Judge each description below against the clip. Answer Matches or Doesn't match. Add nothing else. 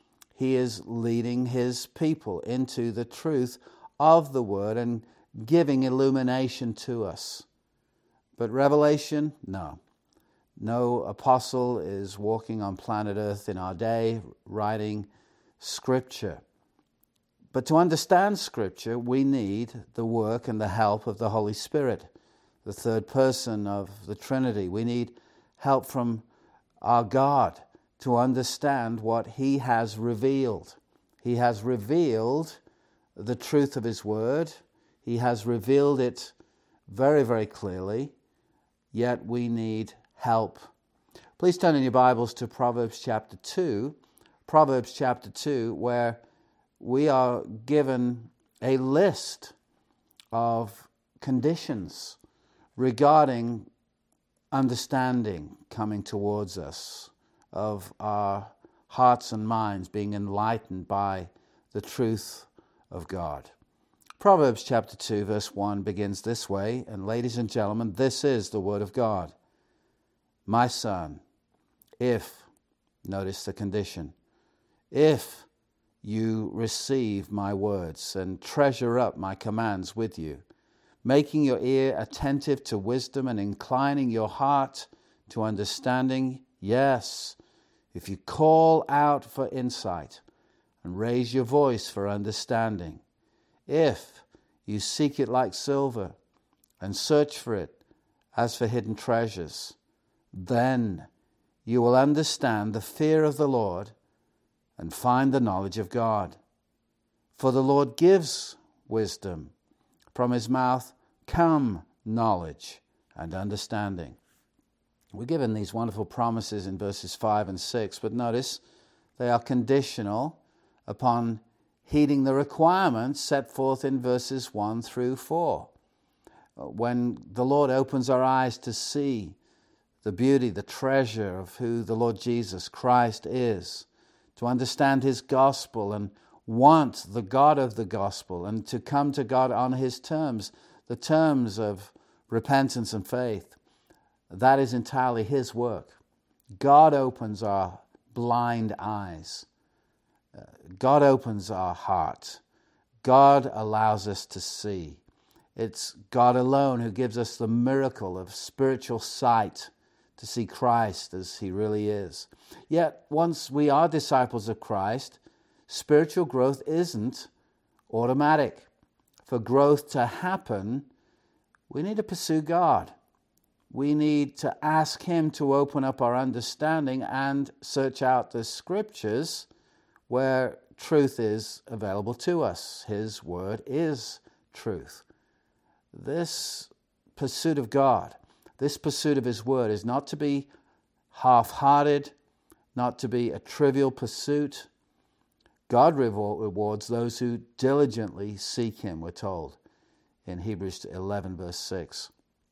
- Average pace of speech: Doesn't match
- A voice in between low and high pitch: Doesn't match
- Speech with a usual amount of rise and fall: Matches